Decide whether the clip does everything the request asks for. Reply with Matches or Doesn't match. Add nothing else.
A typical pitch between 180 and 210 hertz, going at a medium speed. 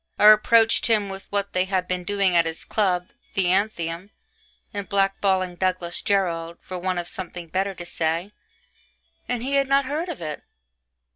Matches